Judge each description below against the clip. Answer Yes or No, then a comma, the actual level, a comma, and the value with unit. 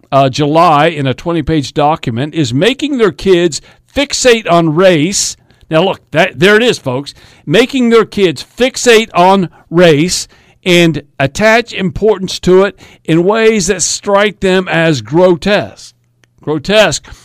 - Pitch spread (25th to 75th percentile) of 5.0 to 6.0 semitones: Yes, wide, 5.6 semitones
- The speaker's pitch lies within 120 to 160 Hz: No, medium, 175 Hz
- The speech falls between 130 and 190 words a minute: Yes, average, 140 wpm